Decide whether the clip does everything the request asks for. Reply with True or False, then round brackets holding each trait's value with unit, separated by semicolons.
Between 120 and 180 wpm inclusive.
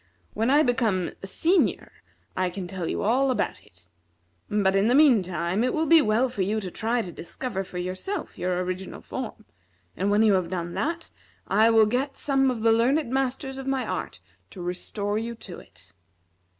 False (190 wpm)